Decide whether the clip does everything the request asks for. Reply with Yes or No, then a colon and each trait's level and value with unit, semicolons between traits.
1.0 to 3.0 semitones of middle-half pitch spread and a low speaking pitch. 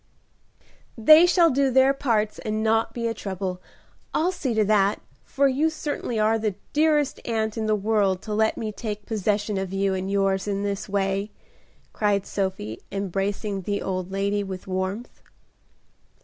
No: average, 2.7 semitones; high, 210 Hz